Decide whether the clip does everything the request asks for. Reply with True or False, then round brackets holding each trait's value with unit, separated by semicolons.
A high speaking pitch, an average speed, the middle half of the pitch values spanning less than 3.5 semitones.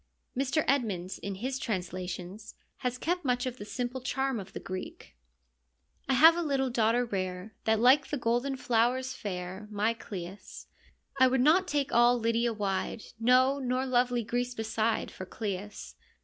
False (240 Hz; 160 wpm; 4.0 semitones)